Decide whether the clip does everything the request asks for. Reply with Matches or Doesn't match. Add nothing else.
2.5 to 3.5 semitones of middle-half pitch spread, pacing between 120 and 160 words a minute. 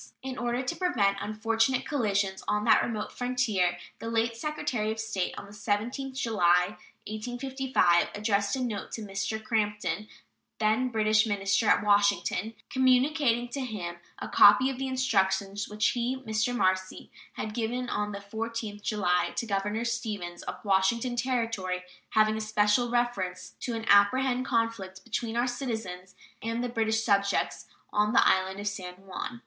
Matches